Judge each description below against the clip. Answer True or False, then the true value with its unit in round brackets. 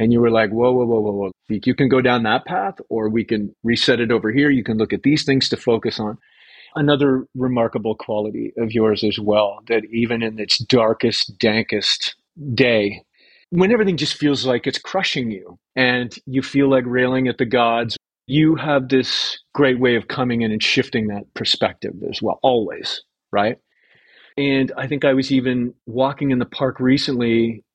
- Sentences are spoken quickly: False (190 wpm)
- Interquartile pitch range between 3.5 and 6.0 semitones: False (3.1 semitones)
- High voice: False (125 Hz)